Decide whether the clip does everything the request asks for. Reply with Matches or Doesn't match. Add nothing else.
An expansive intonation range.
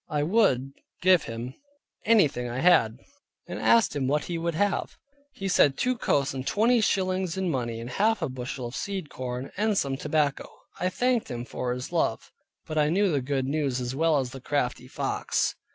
Matches